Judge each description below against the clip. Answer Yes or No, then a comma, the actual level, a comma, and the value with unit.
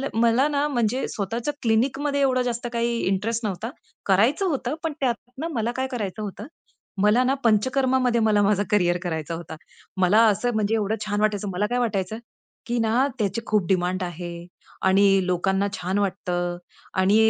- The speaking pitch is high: Yes, high, 215 Hz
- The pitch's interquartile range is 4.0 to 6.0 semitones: Yes, average, 4.3 semitones